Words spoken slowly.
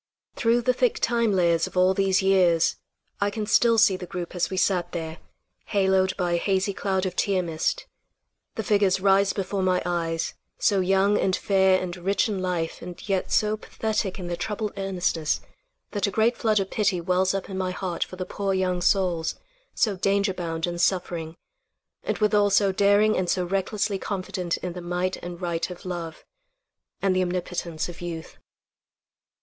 No: average, 185 wpm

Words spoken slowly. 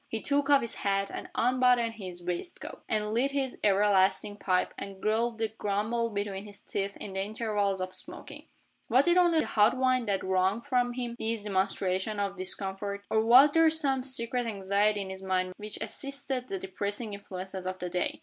No: average, 190 wpm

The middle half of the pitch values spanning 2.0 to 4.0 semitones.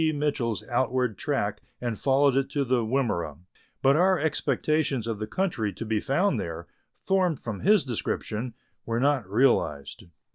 No: average, 4.5 semitones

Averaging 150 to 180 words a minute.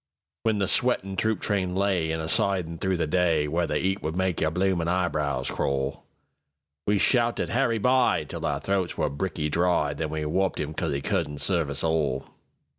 Yes: average, 170 wpm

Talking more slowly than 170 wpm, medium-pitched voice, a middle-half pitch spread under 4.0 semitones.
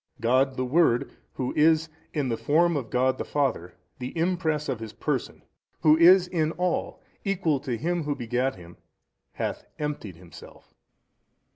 No: average, 160 wpm; medium, 145 Hz; average, 4.7 semitones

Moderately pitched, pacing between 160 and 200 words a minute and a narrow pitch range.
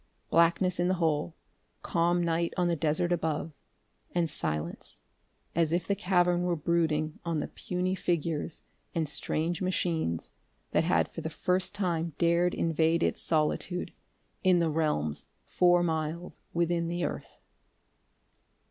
No: medium, 170 Hz; average, 140 wpm; narrow, 1.8 semitones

